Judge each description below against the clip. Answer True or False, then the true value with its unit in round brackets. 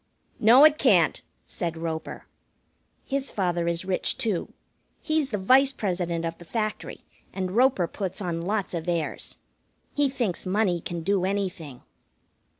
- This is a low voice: False (190 Hz)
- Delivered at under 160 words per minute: True (145 wpm)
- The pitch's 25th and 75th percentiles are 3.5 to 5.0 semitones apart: True (4.7 semitones)